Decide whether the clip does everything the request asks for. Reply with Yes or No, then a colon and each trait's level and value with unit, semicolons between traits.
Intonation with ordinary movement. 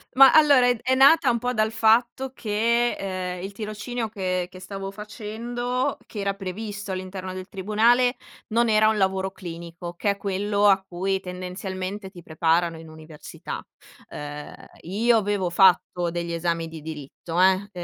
Yes: average, 3.5 semitones